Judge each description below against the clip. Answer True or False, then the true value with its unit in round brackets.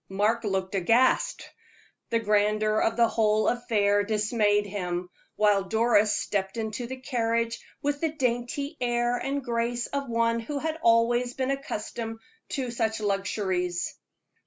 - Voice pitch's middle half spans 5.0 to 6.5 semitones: False (2.8 semitones)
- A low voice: False (230 Hz)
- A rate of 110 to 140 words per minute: True (135 wpm)